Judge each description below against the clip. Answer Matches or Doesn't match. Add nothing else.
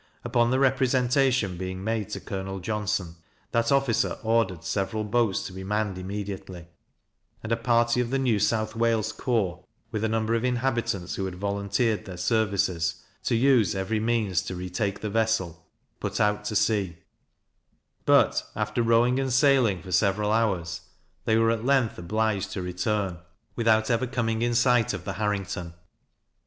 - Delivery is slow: Doesn't match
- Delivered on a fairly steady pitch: Doesn't match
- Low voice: Matches